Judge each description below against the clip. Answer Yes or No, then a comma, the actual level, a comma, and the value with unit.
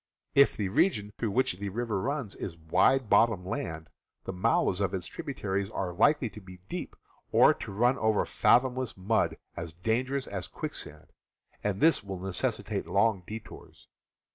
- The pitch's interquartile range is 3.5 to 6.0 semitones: Yes, average, 4.4 semitones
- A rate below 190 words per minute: Yes, average, 165 wpm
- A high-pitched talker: No, low, 100 Hz